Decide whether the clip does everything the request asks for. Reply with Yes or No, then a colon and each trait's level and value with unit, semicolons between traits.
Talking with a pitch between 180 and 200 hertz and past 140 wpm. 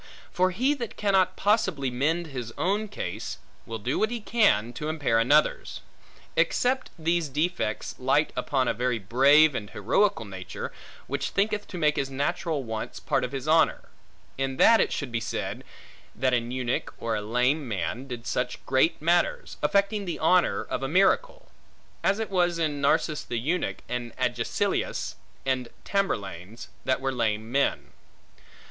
No: medium, 140 Hz; average, 160 wpm